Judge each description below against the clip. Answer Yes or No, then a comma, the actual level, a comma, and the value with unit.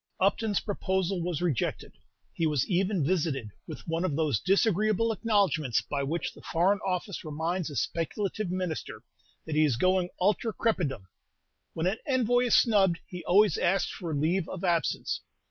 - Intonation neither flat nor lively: Yes, average, 3.8 semitones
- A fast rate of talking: No, average, 160 wpm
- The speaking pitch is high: No, medium, 180 Hz